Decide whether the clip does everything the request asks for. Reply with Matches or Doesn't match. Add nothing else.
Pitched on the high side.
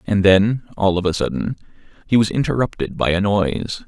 Doesn't match